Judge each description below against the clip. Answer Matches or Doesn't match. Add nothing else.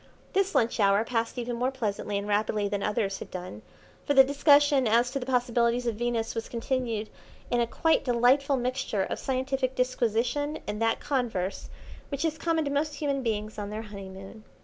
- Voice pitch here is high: Matches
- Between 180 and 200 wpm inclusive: Matches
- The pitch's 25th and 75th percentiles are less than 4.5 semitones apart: Matches